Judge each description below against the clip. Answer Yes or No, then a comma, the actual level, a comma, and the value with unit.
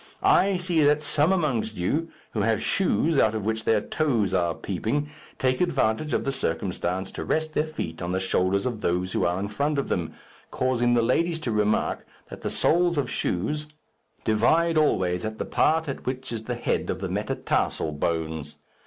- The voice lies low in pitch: Yes, low, 115 Hz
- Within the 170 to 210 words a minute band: Yes, average, 190 wpm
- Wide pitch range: Yes, wide, 8.1 semitones